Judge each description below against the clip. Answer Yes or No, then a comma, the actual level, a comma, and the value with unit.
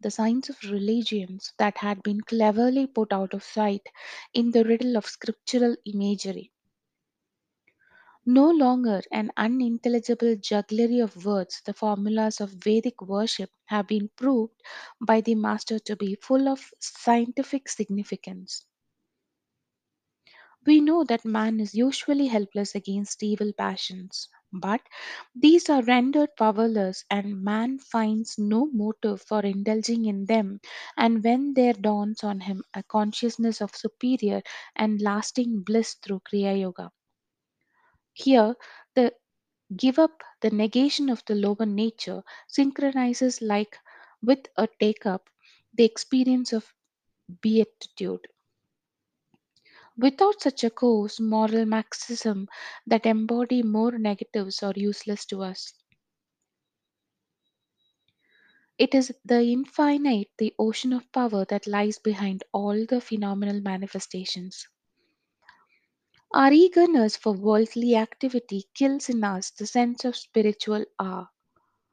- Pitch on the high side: Yes, high, 220 Hz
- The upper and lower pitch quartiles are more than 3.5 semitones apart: No, average, 3.1 semitones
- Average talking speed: No, slow, 120 wpm